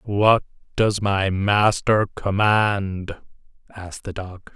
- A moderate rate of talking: No, slow, 105 wpm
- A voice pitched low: Yes, low, 100 Hz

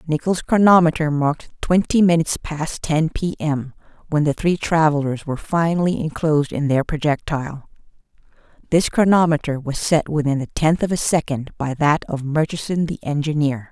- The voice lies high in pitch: No, medium, 155 Hz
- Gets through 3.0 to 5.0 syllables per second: No, 5.2 syllables/s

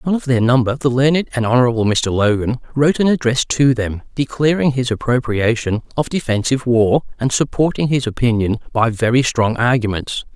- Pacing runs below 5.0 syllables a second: No, 5.6 syllables/s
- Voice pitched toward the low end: Yes, low, 125 Hz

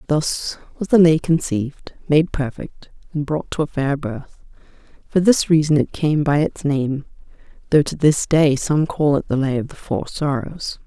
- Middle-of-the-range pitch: Yes, medium, 150 Hz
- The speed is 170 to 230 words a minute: Yes, average, 190 wpm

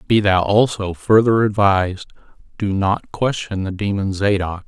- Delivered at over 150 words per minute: No, average, 140 wpm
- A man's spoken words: Yes, male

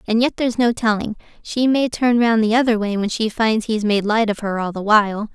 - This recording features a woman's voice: Yes, female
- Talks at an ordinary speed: No, fast, 245 wpm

